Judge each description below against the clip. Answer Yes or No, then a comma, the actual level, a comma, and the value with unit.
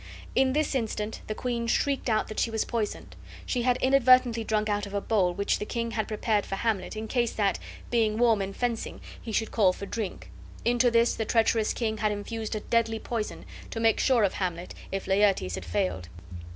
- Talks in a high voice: Yes, high, 220 Hz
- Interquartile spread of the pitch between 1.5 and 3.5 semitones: Yes, narrow, 2.4 semitones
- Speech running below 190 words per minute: No, fast, 205 wpm